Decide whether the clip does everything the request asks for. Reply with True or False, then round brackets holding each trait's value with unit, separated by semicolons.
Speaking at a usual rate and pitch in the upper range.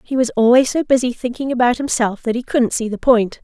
False (245 wpm; 245 Hz)